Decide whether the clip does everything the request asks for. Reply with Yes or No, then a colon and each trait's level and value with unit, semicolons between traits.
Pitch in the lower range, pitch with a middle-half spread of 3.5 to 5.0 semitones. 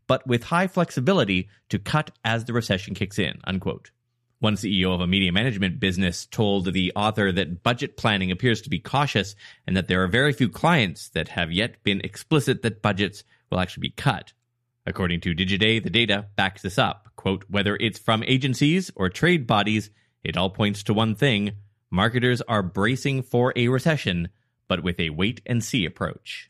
Yes: low, 105 Hz; average, 4.1 semitones